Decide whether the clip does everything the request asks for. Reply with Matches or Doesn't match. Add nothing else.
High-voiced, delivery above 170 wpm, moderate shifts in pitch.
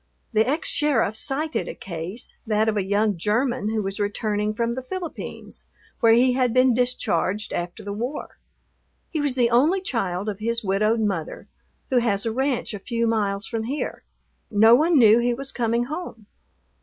Matches